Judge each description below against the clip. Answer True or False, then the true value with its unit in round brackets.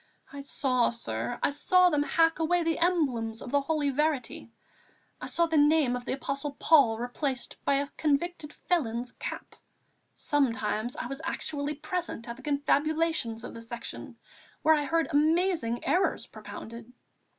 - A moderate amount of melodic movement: True (4.7 semitones)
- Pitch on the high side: True (285 Hz)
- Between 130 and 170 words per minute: True (155 wpm)